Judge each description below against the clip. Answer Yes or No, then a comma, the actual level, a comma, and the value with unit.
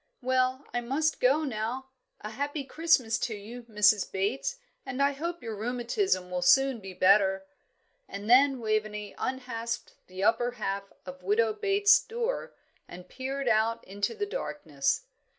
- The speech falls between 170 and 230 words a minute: No, average, 150 wpm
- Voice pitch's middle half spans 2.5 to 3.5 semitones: No, average, 4.9 semitones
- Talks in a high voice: Yes, high, 235 Hz